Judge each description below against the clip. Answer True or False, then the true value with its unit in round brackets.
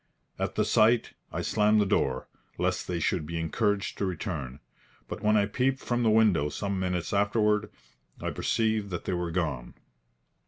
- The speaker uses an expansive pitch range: False (4.1 semitones)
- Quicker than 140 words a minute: True (170 wpm)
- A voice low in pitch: True (100 Hz)